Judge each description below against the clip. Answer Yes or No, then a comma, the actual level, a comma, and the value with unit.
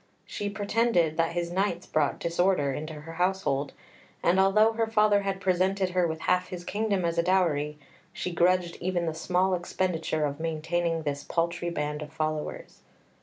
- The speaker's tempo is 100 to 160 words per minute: No, average, 170 wpm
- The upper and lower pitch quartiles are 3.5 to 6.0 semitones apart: No, average, 3.0 semitones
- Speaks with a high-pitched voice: No, medium, 175 Hz